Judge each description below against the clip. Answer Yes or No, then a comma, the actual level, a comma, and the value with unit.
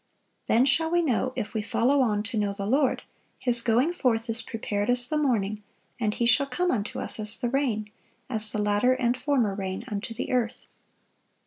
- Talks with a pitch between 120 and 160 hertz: No, high, 235 Hz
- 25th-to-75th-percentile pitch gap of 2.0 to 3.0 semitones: No, average, 3.5 semitones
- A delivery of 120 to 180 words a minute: No, average, 200 wpm